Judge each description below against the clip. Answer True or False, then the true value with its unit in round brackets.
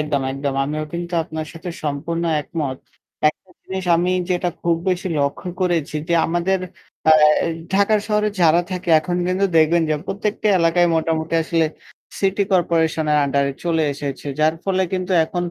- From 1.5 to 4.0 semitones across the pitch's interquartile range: True (2.9 semitones)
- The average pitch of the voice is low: False (170 Hz)